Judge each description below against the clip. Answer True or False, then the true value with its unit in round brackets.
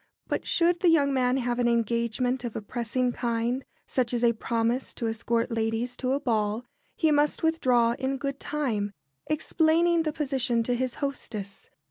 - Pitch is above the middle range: True (250 Hz)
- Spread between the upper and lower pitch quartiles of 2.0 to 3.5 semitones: True (3.2 semitones)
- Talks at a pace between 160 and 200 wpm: True (170 wpm)